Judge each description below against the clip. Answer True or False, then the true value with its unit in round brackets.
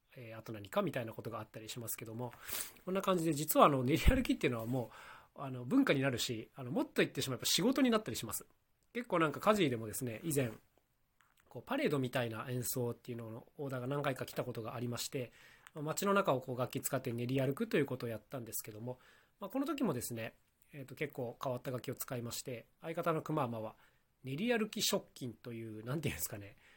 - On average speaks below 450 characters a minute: False (465 characters per minute)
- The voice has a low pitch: True (130 Hz)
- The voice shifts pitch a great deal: False (4.9 semitones)